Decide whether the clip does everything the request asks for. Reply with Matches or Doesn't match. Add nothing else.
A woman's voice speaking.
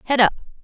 Matches